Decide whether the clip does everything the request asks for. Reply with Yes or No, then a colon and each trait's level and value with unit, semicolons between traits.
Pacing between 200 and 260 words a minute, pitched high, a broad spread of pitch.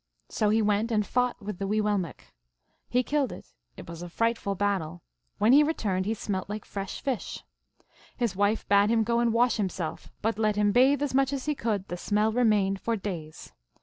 No: fast, 205 wpm; high, 210 Hz; average, 3.1 semitones